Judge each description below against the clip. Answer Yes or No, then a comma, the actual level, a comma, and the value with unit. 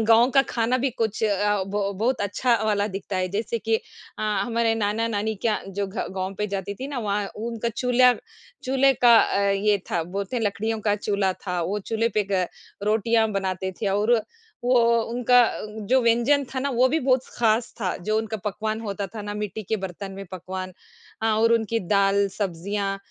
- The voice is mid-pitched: No, high, 215 Hz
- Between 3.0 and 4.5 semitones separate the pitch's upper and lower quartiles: No, narrow, 2.6 semitones